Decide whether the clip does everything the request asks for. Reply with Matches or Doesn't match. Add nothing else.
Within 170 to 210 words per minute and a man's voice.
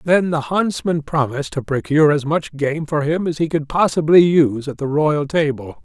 Matches